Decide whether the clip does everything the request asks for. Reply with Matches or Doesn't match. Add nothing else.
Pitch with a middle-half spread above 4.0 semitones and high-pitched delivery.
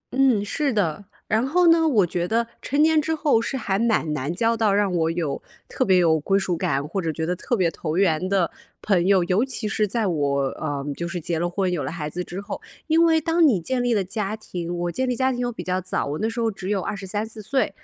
Matches